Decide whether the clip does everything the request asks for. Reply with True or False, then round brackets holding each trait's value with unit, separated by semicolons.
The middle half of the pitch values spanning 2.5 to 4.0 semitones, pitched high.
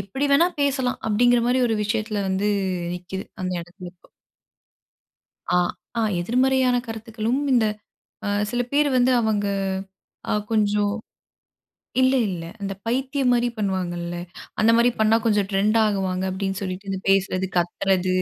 False (4.4 semitones; 210 Hz)